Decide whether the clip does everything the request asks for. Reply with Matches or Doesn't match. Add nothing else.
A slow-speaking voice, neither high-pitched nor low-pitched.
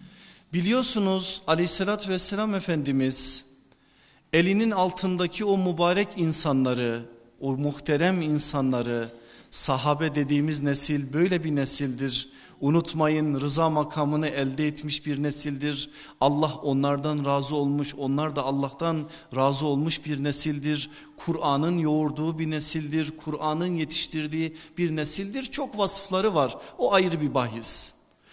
Doesn't match